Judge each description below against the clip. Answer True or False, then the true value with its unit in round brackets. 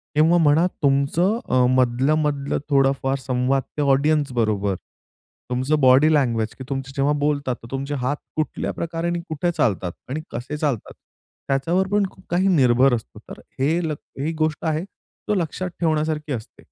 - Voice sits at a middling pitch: True (145 Hz)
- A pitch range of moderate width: True (3.3 semitones)